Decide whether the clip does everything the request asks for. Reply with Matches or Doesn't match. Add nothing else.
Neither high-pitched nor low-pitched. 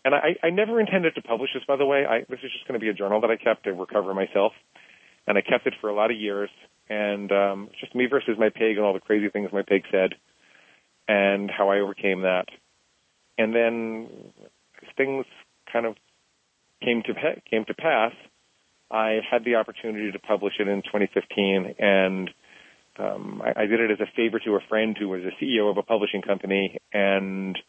Doesn't match